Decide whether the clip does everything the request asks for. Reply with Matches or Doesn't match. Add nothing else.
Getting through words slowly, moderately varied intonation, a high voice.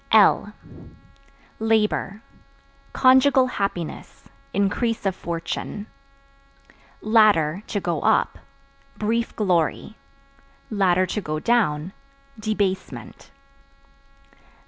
Matches